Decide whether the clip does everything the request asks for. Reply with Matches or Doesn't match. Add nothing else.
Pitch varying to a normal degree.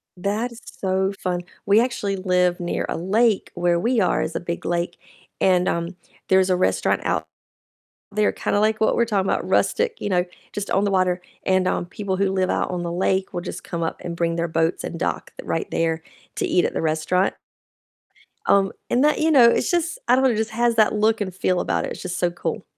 Matches